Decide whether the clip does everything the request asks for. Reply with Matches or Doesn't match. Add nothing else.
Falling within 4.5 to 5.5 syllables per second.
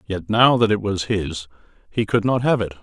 Matches